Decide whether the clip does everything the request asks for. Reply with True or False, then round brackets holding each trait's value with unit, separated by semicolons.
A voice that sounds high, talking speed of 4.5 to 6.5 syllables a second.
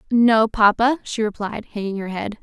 True (220 Hz; 4.7 syllables/s)